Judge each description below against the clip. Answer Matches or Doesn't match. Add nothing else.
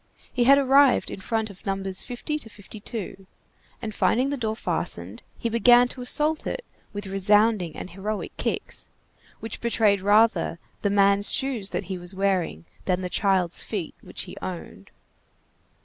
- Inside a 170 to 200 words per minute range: Doesn't match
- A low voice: Doesn't match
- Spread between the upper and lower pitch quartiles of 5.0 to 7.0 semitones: Doesn't match